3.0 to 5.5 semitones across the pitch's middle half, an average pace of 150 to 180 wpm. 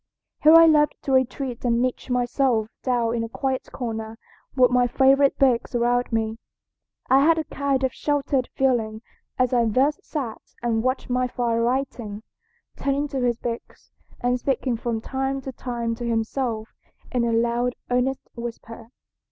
No: narrow, 2.4 semitones; average, 160 wpm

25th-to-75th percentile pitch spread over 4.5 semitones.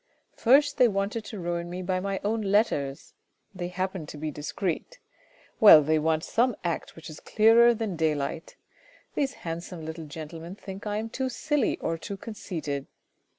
Yes: average, 5.2 semitones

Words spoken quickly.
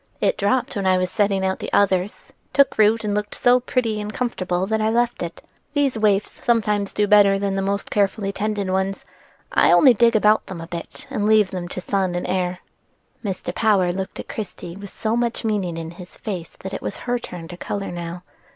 Yes: fast, 215 wpm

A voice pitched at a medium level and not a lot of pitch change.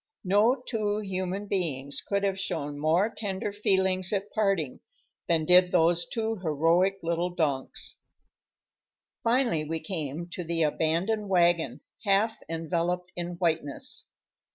No: medium, 180 Hz; average, 3.4 semitones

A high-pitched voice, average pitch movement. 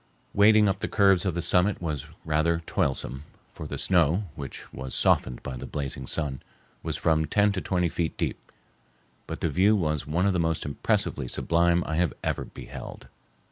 No: very low, 85 Hz; average, 3.7 semitones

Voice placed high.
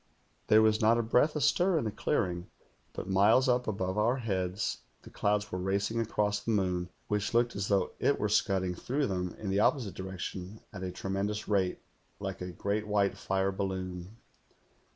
No: low, 100 Hz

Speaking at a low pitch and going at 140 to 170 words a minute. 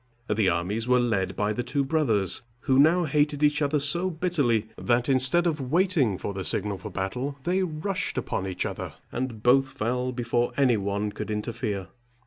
No: low, 125 Hz; average, 180 wpm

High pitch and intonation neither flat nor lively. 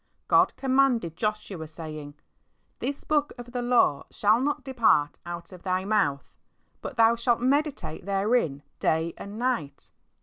No: high, 215 Hz; wide, 7.2 semitones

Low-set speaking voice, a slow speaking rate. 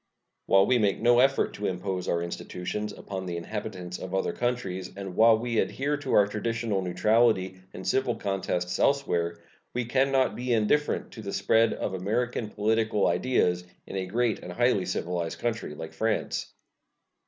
No: low, 105 Hz; average, 165 wpm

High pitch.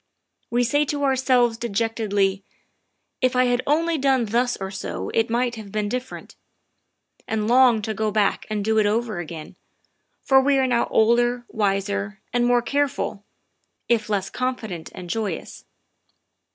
Yes: high, 230 Hz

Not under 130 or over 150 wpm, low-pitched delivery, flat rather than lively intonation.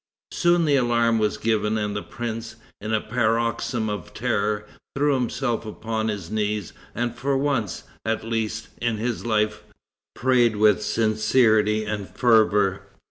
Yes: average, 140 wpm; low, 110 Hz; narrow, 2.0 semitones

